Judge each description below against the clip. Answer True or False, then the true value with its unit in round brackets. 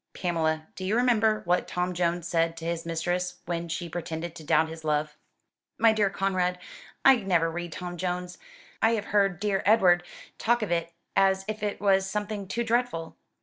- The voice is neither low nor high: True (180 Hz)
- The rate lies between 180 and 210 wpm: True (185 wpm)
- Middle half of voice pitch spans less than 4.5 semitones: True (3.5 semitones)